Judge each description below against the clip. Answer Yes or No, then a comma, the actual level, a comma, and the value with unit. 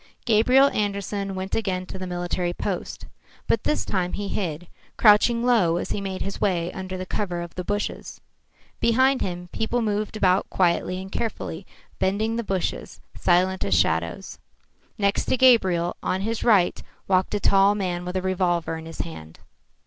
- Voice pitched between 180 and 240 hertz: Yes, high, 190 Hz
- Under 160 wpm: No, average, 170 wpm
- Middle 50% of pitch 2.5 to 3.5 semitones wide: Yes, average, 3.0 semitones